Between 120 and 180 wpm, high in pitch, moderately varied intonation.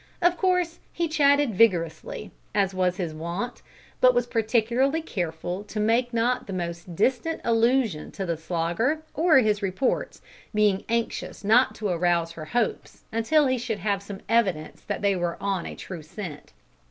No: average, 165 wpm; high, 210 Hz; wide, 5.8 semitones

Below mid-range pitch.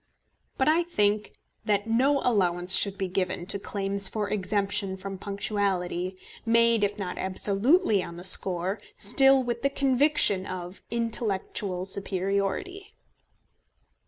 No: high, 200 Hz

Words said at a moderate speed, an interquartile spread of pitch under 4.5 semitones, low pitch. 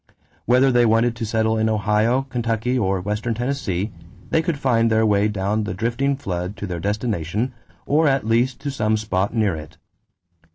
Yes: average, 175 wpm; average, 3.1 semitones; low, 110 Hz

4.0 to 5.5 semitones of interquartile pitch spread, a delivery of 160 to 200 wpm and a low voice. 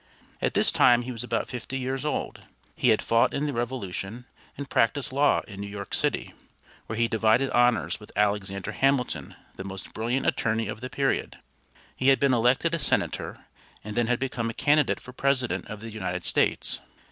No: average, 3.5 semitones; average, 190 wpm; low, 120 Hz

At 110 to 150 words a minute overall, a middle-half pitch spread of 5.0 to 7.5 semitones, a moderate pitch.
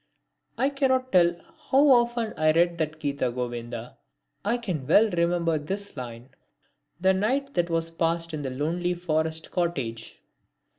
Yes: average, 145 wpm; average, 5.3 semitones; medium, 170 Hz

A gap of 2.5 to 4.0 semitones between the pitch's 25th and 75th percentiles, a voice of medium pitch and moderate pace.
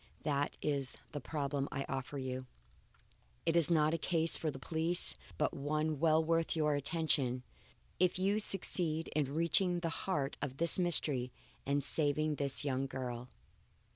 Yes: average, 3.2 semitones; medium, 150 Hz; average, 155 wpm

